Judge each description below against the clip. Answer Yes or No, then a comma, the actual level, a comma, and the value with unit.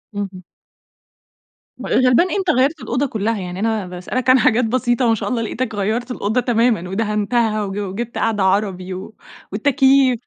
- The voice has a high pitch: Yes, high, 225 Hz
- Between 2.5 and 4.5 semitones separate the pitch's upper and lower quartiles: Yes, average, 3.7 semitones